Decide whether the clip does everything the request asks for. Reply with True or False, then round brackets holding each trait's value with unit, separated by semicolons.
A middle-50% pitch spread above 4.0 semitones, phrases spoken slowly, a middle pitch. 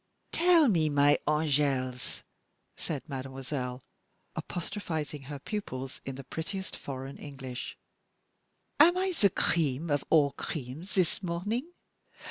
True (5.2 semitones; 110 wpm; 150 Hz)